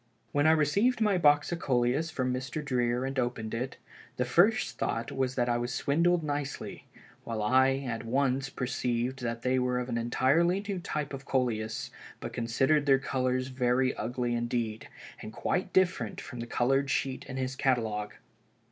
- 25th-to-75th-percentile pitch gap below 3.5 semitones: Yes, average, 3.0 semitones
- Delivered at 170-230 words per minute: Yes, average, 175 wpm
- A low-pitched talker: Yes, low, 130 Hz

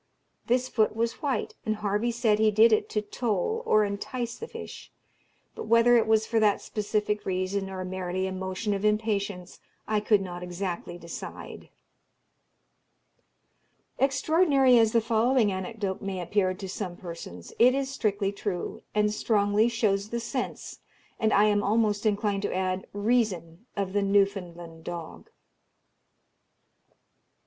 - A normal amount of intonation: Yes, average, 3.1 semitones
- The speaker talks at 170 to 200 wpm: No, average, 145 wpm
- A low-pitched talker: No, high, 210 Hz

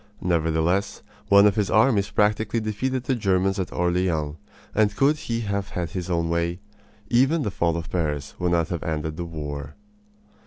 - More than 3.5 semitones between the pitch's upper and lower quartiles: Yes, average, 4.1 semitones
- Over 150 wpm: Yes, average, 170 wpm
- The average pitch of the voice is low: Yes, very low, 90 Hz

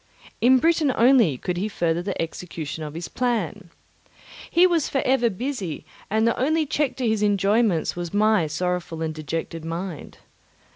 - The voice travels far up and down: Yes, wide, 7.0 semitones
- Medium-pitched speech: No, high, 200 Hz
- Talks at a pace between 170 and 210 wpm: No, average, 160 wpm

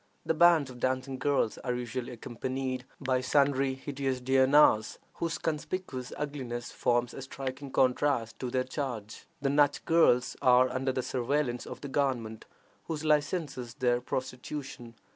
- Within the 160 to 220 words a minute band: No, average, 145 wpm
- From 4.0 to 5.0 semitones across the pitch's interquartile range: No, narrow, 2.5 semitones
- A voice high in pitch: No, low, 130 Hz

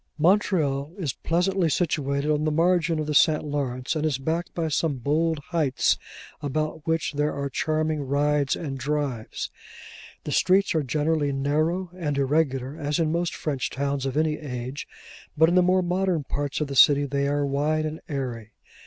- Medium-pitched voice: Yes, medium, 150 Hz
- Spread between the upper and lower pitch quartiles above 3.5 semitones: No, narrow, 2.5 semitones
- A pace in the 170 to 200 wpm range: Yes, average, 175 wpm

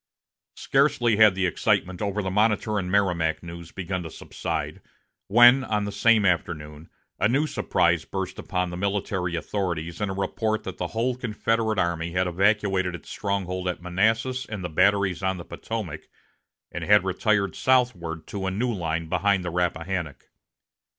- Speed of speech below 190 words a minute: Yes, average, 165 wpm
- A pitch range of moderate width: Yes, average, 3.3 semitones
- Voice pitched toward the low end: Yes, very low, 95 Hz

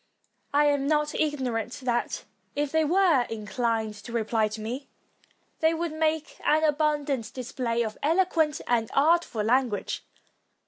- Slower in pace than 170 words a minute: Yes, average, 140 wpm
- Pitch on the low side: No, very high, 275 Hz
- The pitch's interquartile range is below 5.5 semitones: Yes, average, 5.1 semitones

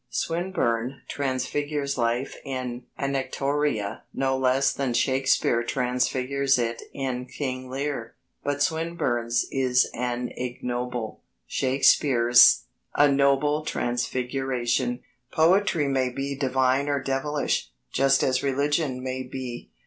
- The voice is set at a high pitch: No, low, 130 Hz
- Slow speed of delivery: Yes, slow, 105 wpm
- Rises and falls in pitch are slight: Yes, narrow, 2.0 semitones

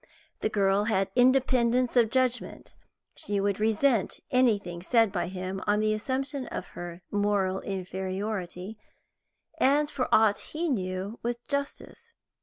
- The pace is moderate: No, slow, 130 wpm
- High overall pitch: Yes, high, 215 Hz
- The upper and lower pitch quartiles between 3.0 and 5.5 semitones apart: Yes, average, 4.7 semitones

